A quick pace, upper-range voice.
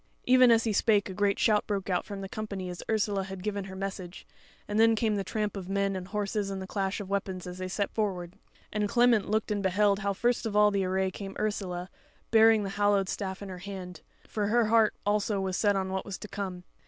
Yes: fast, 240 wpm; high, 200 Hz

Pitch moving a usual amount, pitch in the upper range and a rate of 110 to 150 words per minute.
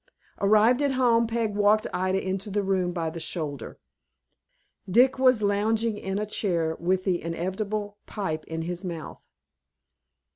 Yes: average, 3.4 semitones; high, 200 Hz; average, 145 wpm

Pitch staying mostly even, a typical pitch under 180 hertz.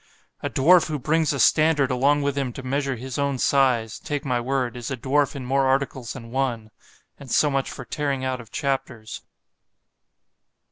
Yes: narrow, 2.0 semitones; low, 135 Hz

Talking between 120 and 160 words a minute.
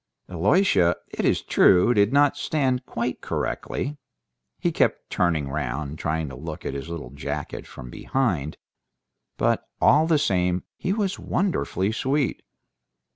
Yes: slow, 135 wpm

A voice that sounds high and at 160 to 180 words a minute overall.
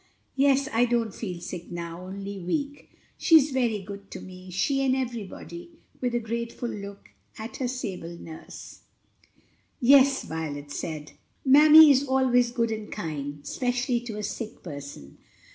No: high, 230 Hz; average, 145 wpm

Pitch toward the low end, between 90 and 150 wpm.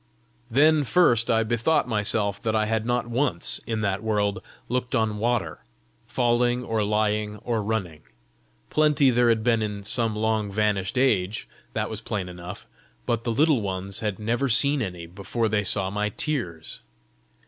No: low, 110 Hz; average, 160 wpm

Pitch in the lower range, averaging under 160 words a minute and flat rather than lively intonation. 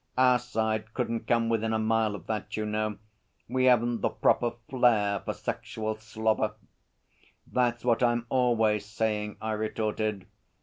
Yes: low, 110 Hz; average, 145 wpm; narrow, 1.7 semitones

